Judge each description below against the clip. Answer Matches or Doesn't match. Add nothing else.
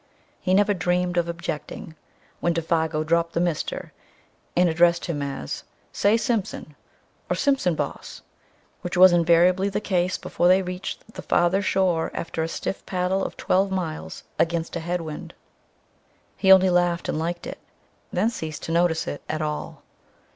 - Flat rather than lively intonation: Matches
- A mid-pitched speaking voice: Matches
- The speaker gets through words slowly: Doesn't match